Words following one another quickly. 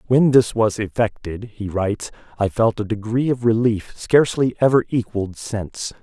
No: average, 160 wpm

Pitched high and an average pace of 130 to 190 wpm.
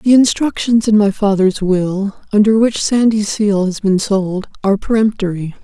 Yes: high, 205 Hz; average, 150 wpm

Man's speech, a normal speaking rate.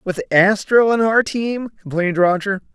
Yes: male; average, 155 wpm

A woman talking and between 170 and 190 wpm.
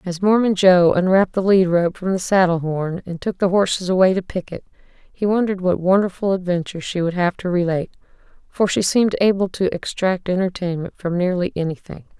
Yes: female; average, 185 wpm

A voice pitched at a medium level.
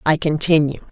Yes: medium, 155 Hz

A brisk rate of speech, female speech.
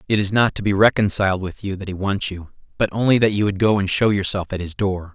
No: fast, 280 wpm; male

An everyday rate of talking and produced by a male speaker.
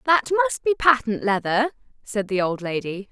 No: average, 175 wpm; female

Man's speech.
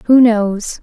No: female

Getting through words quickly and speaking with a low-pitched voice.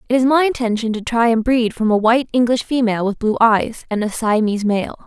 No: fast, 235 wpm; high, 230 Hz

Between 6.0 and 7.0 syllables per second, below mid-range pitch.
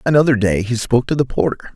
Yes: 6.7 syllables/s; low, 125 Hz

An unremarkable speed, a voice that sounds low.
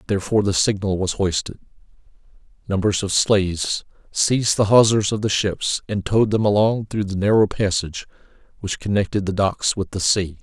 Yes: average, 165 wpm; low, 100 Hz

